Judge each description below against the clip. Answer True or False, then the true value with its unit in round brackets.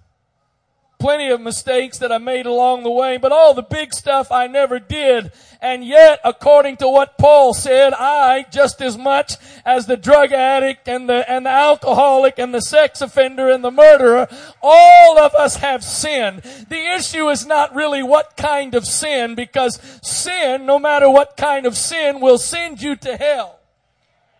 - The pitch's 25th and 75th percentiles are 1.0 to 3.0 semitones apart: True (2.6 semitones)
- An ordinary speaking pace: True (175 wpm)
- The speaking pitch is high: True (270 Hz)